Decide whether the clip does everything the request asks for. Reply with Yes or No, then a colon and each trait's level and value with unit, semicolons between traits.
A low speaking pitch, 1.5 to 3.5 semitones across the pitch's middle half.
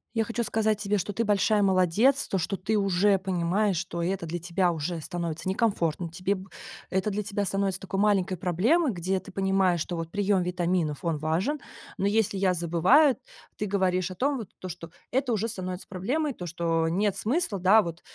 No: high, 190 Hz; average, 3.1 semitones